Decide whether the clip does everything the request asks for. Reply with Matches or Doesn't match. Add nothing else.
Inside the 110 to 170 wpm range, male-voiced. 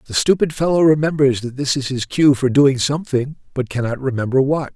Doesn't match